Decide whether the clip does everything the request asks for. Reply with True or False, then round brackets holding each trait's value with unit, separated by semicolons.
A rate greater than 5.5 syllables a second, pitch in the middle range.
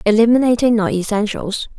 False (5.7 syllables/s; 225 Hz)